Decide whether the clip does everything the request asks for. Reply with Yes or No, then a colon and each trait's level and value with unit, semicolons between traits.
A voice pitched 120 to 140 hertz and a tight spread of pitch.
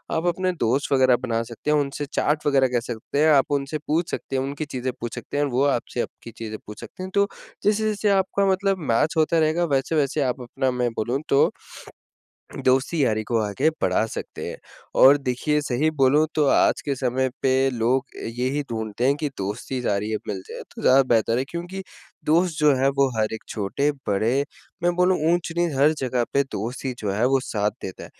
No: low, 135 Hz; average, 4.2 semitones